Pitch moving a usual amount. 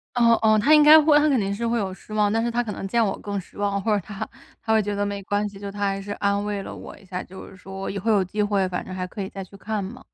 No: narrow, 2.2 semitones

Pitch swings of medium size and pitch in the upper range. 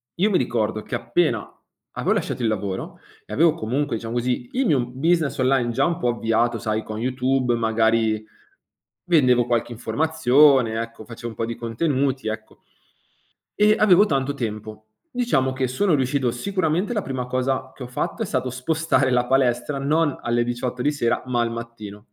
No: average, 3.8 semitones; low, 125 Hz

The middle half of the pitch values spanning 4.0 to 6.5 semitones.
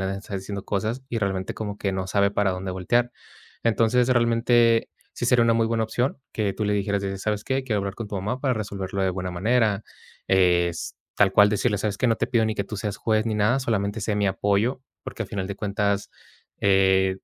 No: average, 2.8 semitones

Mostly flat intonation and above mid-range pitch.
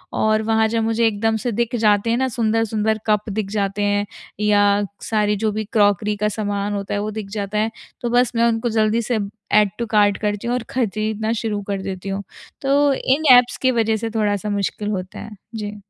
Yes: narrow, 1.8 semitones; high, 215 Hz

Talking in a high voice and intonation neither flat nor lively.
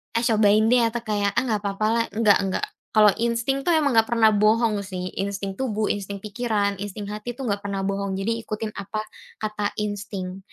No: high, 210 Hz; narrow, 2.2 semitones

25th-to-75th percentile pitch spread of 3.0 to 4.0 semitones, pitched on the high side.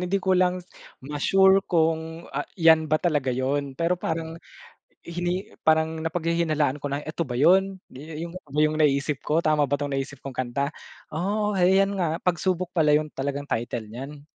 No: average, 3.6 semitones; medium, 160 Hz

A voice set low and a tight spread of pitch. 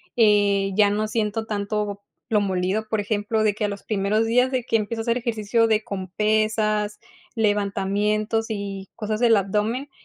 No: high, 210 Hz; narrow, 1.6 semitones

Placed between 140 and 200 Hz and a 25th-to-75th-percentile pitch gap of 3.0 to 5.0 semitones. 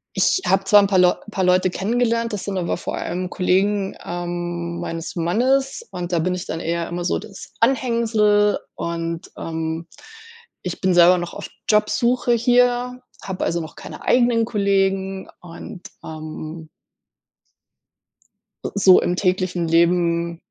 Yes: medium, 185 Hz; average, 3.7 semitones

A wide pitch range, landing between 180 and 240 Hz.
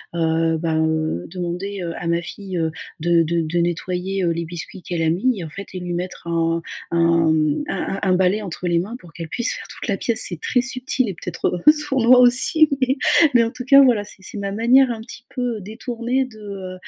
Yes: wide, 5.8 semitones; medium, 185 Hz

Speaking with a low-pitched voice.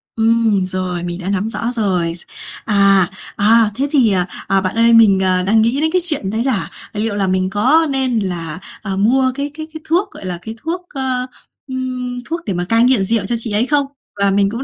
No: high, 220 Hz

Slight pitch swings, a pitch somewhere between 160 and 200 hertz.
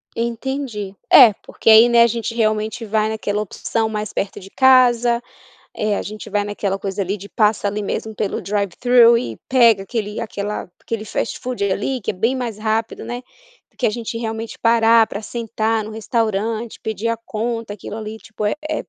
No: narrow, 1.9 semitones; high, 220 Hz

